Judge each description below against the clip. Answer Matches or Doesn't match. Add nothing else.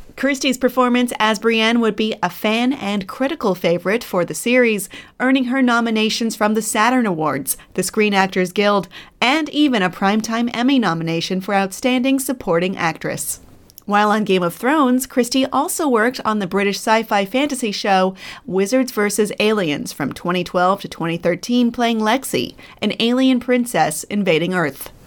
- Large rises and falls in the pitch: Doesn't match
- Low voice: Doesn't match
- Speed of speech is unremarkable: Matches